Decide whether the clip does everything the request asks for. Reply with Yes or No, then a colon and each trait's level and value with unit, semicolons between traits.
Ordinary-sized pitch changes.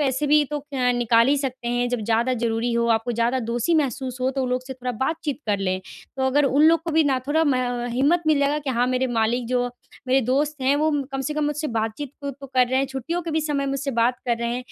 Yes: average, 3.2 semitones